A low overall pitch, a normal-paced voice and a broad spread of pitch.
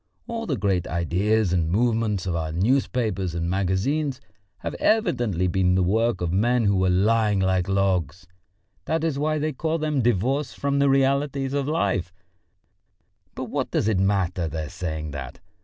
Yes: low, 100 Hz; average, 165 wpm; wide, 7.0 semitones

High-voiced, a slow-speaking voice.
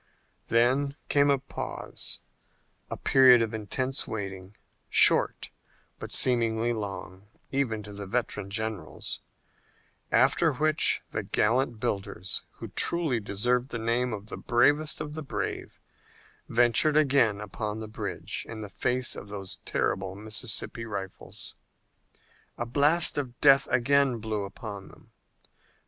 No: low, 115 Hz; slow, 130 wpm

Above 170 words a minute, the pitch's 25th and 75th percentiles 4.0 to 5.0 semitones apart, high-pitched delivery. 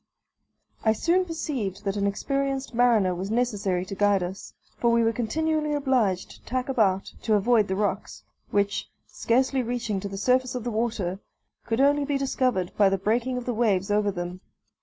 Yes: average, 180 wpm; average, 4.5 semitones; high, 225 Hz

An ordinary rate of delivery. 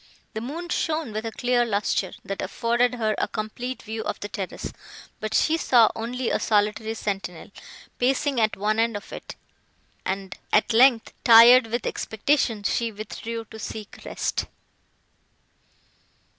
Yes: average, 145 wpm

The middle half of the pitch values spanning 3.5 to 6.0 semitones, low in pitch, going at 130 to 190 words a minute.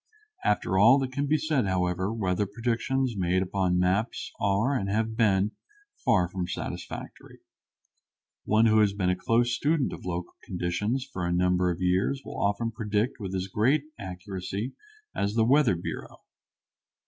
Yes: average, 4.2 semitones; low, 100 Hz; average, 160 wpm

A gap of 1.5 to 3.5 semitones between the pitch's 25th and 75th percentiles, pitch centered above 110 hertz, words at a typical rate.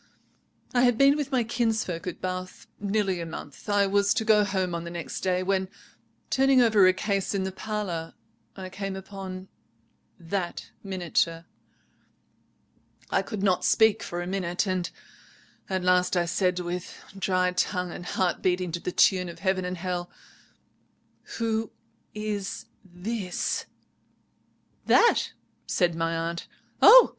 Yes: average, 2.7 semitones; high, 190 Hz; average, 145 wpm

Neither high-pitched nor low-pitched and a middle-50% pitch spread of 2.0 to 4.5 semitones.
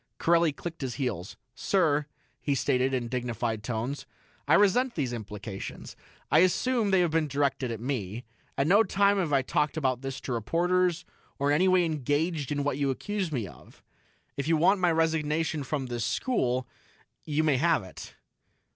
No: medium, 145 Hz; average, 5.1 semitones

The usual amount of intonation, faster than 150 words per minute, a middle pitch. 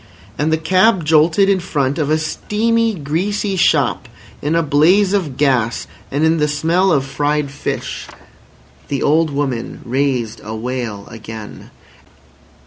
No: average, 4.4 semitones; average, 140 wpm; medium, 150 Hz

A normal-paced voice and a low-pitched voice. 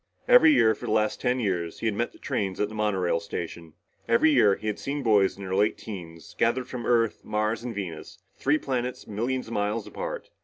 No: fast, 220 wpm; low, 110 Hz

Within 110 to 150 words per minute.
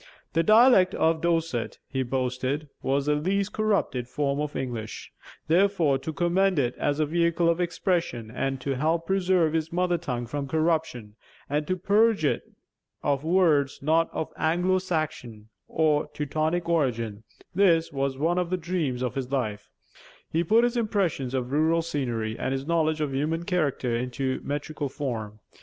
No: average, 160 wpm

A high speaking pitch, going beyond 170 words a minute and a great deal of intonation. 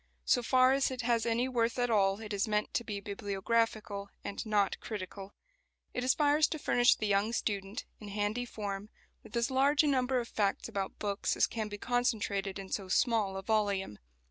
No: high, 215 Hz; average, 195 wpm; average, 3.4 semitones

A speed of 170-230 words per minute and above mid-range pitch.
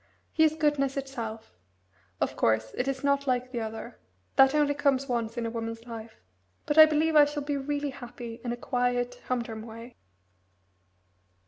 Yes: average, 175 wpm; very high, 250 Hz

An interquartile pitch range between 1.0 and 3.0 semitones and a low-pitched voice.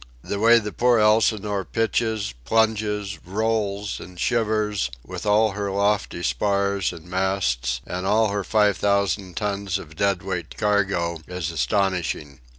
Yes: narrow, 2.6 semitones; low, 100 Hz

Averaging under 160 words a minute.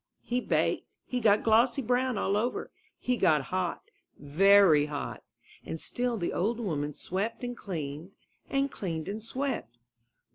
Yes: average, 150 wpm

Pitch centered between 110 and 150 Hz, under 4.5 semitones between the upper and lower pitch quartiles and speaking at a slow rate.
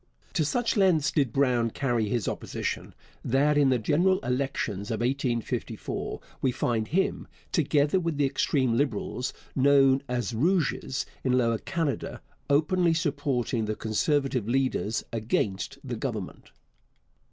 Yes: low, 135 Hz; average, 3.9 semitones; slow, 130 wpm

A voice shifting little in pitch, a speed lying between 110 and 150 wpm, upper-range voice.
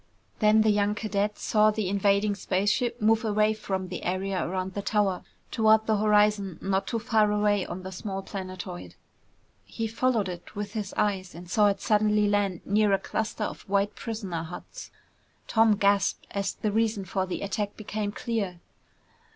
No: narrow, 2.0 semitones; average, 170 wpm; high, 205 Hz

